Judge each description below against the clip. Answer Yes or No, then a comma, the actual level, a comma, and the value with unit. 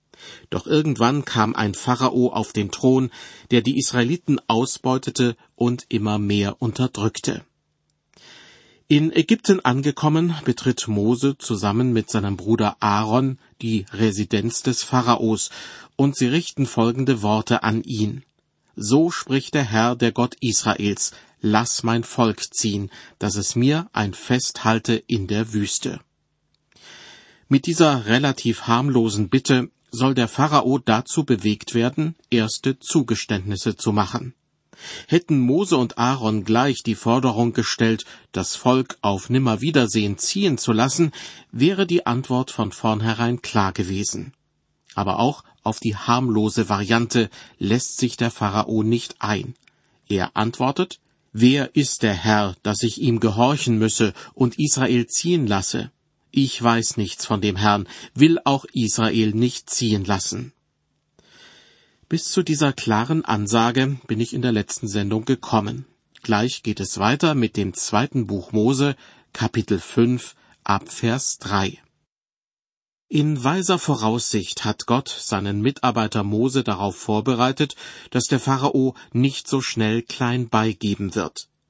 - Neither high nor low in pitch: No, low, 120 Hz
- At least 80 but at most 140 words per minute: Yes, average, 130 wpm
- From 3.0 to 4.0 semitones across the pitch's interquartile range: Yes, average, 3.4 semitones